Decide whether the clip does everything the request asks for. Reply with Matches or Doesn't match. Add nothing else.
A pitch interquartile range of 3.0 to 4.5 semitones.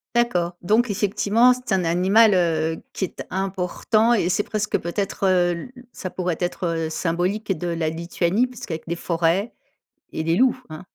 Matches